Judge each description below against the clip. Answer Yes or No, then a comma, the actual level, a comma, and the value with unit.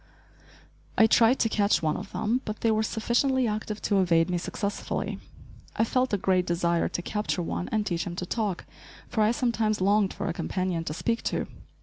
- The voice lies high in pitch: Yes, high, 210 Hz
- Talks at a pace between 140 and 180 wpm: No, average, 200 wpm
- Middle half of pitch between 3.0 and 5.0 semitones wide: Yes, average, 3.7 semitones